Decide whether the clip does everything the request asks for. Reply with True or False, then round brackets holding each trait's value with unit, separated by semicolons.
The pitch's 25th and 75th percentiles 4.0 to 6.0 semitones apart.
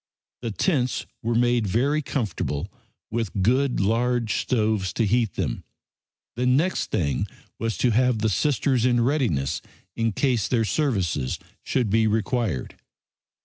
False (3.4 semitones)